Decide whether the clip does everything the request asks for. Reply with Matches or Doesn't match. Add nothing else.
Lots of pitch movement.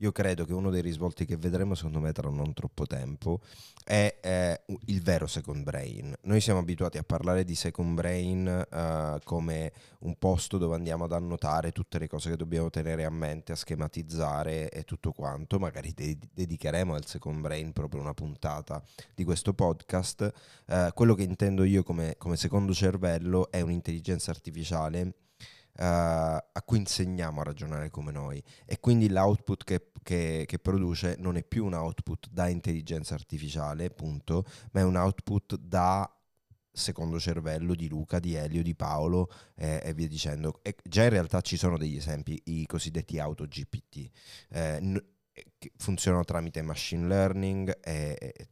Doesn't match